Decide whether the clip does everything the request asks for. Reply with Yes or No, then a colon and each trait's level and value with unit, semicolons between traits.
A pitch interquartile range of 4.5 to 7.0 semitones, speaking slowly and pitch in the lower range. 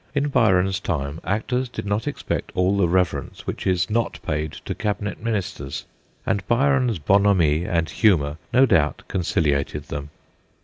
No: wide, 5.6 semitones; average, 145 wpm; very low, 95 Hz